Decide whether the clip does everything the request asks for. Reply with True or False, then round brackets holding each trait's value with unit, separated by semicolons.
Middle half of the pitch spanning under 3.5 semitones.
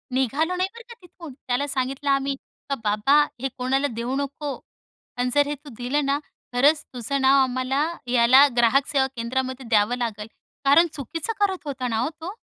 True (2.6 semitones)